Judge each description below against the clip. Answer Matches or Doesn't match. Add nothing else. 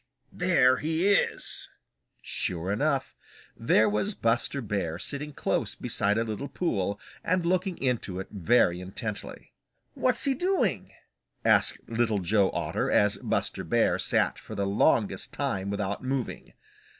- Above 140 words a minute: Doesn't match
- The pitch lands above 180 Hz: Doesn't match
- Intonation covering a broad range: Matches